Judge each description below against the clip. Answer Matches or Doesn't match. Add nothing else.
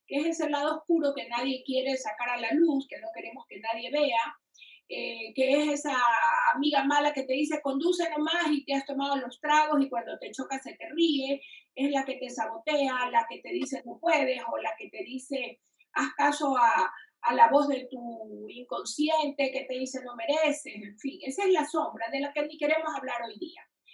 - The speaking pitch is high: Matches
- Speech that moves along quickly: Matches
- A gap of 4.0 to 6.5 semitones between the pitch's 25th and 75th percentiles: Doesn't match